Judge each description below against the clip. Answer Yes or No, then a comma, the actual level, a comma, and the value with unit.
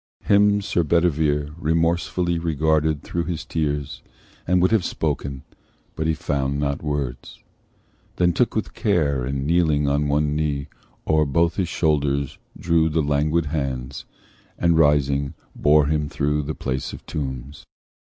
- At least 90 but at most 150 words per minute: Yes, average, 145 wpm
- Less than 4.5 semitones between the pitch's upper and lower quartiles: Yes, average, 2.8 semitones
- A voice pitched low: Yes, very low, 75 Hz